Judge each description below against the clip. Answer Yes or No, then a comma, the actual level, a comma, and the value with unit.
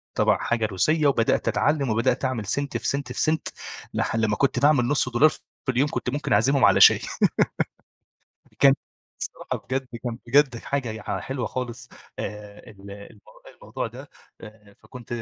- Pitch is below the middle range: Yes, low, 125 Hz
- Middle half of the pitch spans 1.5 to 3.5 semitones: No, average, 3.9 semitones